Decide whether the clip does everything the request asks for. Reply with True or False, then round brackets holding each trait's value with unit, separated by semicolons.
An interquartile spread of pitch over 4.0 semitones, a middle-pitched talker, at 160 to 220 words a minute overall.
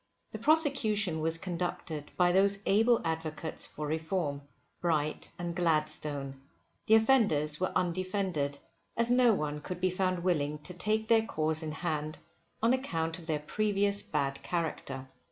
False (4.8 semitones; 175 Hz; 145 wpm)